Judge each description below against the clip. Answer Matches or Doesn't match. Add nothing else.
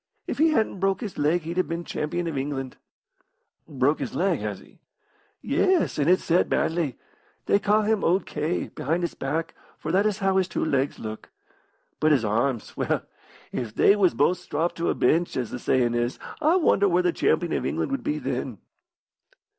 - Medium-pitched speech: Matches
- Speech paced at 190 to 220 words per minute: Matches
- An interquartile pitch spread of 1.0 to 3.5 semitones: Doesn't match